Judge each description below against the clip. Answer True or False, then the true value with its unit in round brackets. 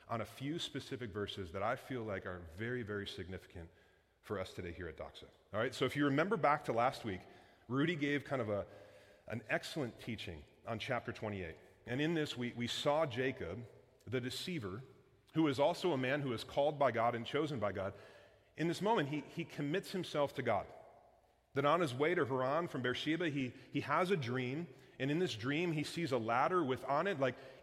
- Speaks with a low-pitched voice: True (130 Hz)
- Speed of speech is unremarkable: False (210 wpm)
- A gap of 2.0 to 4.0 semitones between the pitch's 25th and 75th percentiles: False (4.5 semitones)